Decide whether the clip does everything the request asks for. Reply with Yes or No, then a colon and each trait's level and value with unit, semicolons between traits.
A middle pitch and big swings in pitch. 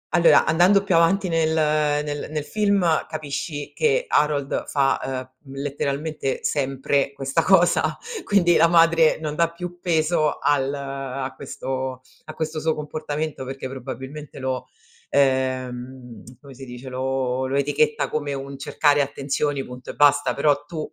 No: medium, 145 Hz; average, 2.8 semitones